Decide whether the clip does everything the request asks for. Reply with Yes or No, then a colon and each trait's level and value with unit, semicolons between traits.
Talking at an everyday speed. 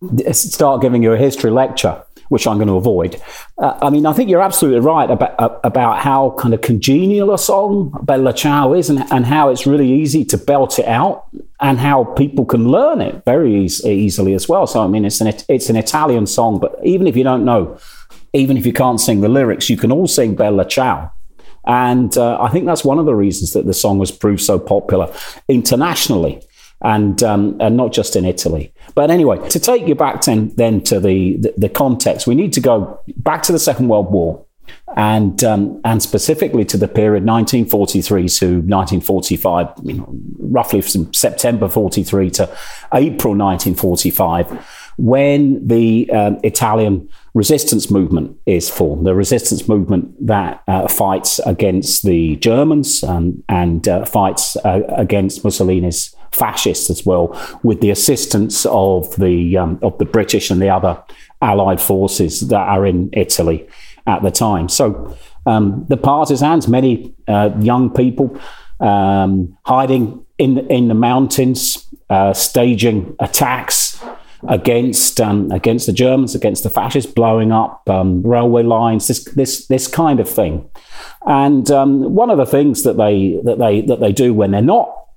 Yes: average, 180 wpm